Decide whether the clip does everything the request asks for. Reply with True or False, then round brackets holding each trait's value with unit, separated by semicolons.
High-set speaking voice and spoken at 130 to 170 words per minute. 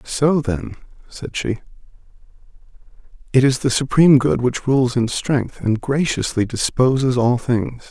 False (130 Hz; 135 wpm)